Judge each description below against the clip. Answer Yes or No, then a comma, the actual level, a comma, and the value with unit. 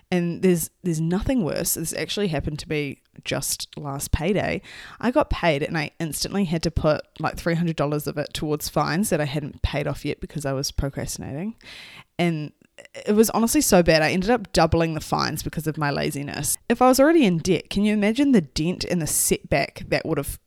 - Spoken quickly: Yes, fast, 215 wpm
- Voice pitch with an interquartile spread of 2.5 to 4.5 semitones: No, average, 4.9 semitones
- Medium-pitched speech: Yes, medium, 165 Hz